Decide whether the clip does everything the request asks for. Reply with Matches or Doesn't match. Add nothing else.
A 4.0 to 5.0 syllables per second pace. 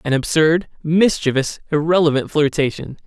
Matches